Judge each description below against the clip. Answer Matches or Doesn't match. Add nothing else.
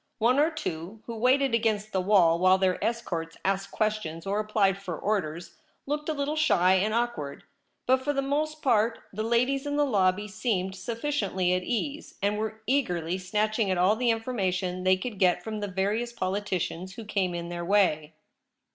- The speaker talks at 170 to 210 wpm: Matches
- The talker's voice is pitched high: Matches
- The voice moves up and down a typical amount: Matches